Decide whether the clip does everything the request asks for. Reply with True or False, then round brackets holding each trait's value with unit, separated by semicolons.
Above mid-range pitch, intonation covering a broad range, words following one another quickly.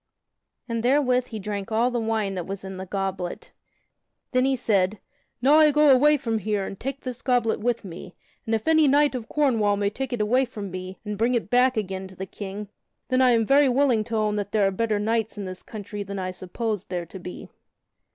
False (220 Hz; 4.3 semitones; 225 wpm)